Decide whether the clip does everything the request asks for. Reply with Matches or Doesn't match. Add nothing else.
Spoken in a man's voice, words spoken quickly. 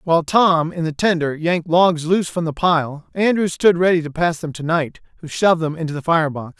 Matches